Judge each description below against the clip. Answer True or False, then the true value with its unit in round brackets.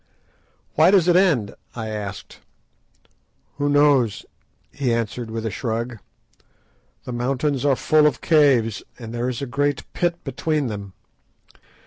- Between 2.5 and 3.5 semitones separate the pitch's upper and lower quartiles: False (4.3 semitones)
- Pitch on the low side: True (125 Hz)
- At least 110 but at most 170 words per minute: True (135 wpm)